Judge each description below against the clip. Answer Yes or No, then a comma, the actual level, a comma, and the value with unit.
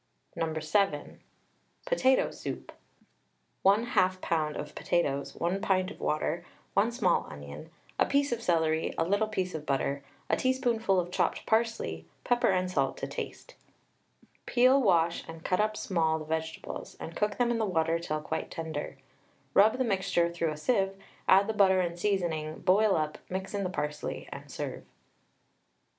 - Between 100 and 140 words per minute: No, average, 160 wpm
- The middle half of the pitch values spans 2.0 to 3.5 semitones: No, average, 4.8 semitones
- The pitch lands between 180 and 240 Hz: Yes, medium, 185 Hz